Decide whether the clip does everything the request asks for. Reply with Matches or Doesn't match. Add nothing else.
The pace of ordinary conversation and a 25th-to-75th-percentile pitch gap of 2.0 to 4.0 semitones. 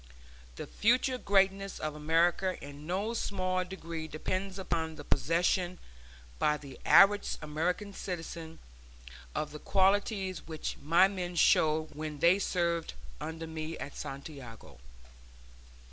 Doesn't match